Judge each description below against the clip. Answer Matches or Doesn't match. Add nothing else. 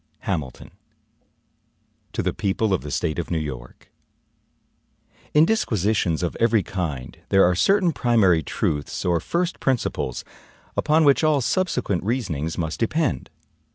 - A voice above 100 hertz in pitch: Doesn't match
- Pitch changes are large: Matches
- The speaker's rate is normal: Doesn't match